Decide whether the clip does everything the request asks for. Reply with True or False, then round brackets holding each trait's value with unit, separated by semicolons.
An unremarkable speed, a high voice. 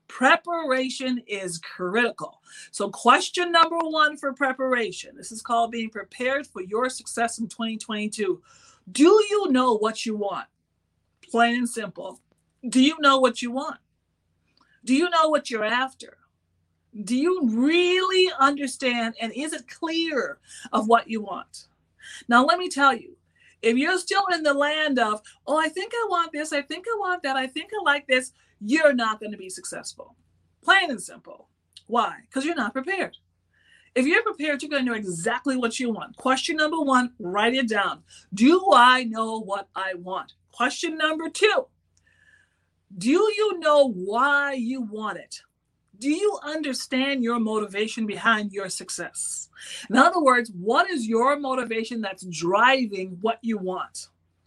True (160 wpm; 255 Hz)